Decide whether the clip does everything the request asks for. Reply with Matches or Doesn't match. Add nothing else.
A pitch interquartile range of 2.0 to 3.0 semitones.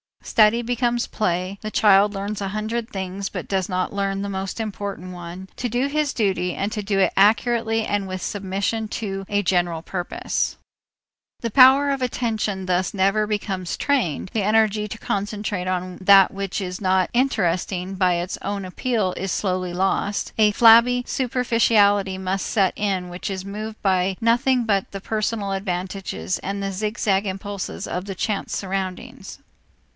Matches